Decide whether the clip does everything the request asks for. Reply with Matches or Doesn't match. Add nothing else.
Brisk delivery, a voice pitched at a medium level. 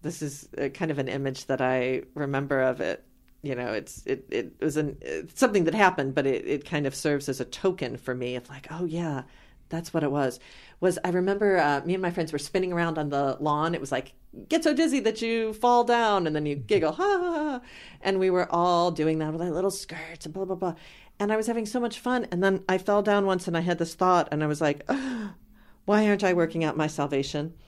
Matches